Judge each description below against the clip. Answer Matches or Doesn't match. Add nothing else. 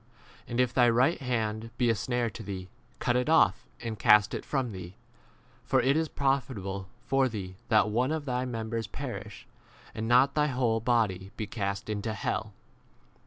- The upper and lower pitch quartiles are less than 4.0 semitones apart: Matches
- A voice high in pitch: Doesn't match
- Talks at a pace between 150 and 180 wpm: Doesn't match